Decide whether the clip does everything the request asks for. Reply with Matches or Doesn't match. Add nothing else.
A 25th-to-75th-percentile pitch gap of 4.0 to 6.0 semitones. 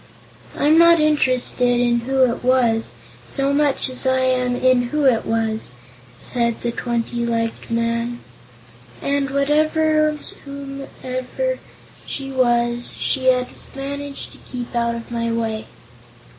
Doesn't match